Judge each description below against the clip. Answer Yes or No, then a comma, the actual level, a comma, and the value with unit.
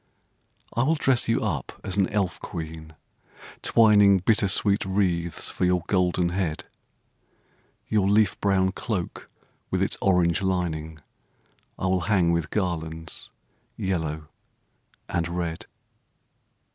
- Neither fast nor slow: No, slow, 115 wpm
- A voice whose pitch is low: Yes, very low, 90 Hz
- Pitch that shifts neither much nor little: Yes, average, 3.0 semitones